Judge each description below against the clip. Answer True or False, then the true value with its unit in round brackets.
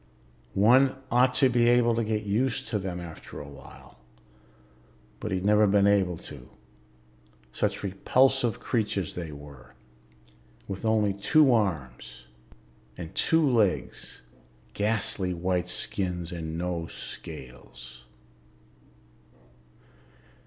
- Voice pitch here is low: True (100 Hz)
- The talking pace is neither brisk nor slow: False (110 wpm)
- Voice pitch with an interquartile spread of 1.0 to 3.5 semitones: False (5.2 semitones)